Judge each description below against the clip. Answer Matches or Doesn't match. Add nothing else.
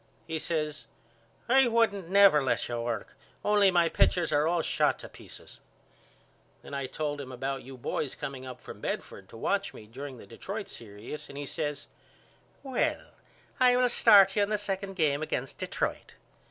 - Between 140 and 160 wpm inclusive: Doesn't match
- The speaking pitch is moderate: Matches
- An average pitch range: Doesn't match